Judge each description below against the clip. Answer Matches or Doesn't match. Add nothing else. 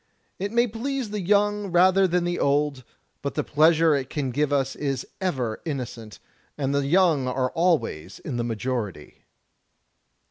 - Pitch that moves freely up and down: Matches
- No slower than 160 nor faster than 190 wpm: Doesn't match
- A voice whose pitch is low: Doesn't match